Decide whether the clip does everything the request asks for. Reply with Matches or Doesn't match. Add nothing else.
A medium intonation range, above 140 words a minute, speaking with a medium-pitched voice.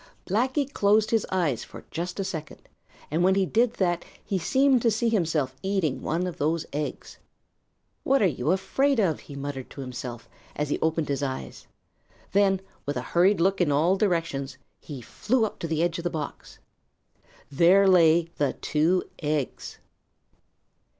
Matches